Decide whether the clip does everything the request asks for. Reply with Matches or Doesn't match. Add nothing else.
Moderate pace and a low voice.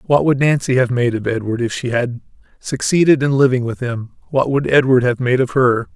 Doesn't match